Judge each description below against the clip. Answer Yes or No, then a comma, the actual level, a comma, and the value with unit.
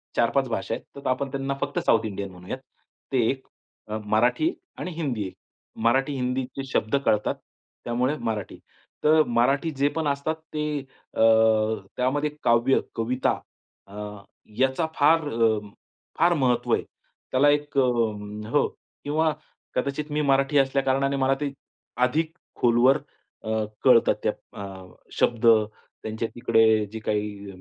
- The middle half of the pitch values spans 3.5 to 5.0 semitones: Yes, average, 4.1 semitones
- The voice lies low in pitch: Yes, low, 130 Hz